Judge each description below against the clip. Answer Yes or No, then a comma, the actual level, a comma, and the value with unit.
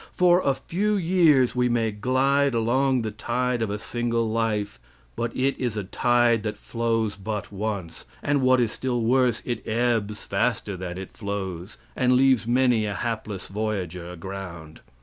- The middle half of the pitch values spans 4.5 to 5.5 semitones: No, average, 3.7 semitones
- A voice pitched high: No, low, 115 Hz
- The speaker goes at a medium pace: Yes, average, 165 wpm